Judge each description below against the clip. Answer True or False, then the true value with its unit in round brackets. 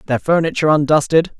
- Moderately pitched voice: True (155 Hz)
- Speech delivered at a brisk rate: False (130 wpm)